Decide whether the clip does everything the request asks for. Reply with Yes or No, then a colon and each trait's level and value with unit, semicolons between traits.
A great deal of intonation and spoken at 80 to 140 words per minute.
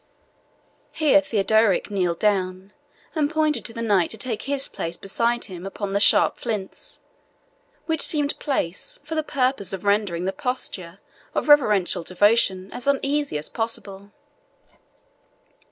Yes: wide, 6.3 semitones; slow, 135 wpm